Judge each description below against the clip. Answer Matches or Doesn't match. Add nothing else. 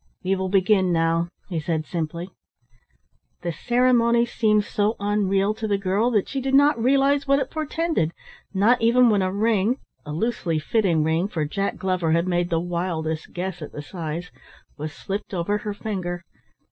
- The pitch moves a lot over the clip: Doesn't match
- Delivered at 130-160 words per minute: Doesn't match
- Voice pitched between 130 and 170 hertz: Doesn't match